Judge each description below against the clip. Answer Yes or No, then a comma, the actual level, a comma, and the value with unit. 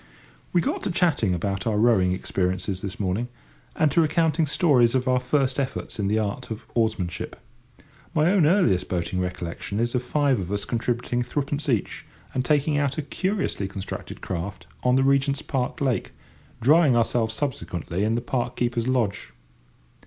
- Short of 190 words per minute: Yes, average, 165 wpm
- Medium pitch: No, low, 120 Hz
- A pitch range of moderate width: No, wide, 5.9 semitones